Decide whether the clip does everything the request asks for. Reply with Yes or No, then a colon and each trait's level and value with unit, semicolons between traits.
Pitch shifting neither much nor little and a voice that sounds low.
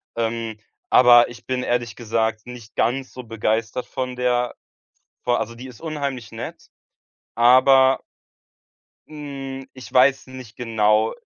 No: narrow, 2.2 semitones; low, 125 Hz